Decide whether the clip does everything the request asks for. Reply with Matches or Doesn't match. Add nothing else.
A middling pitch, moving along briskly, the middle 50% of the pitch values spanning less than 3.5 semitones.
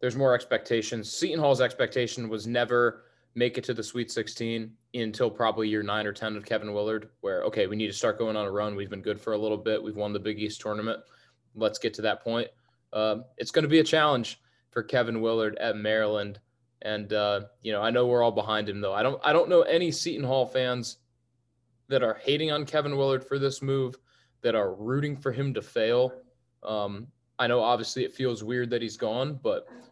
Doesn't match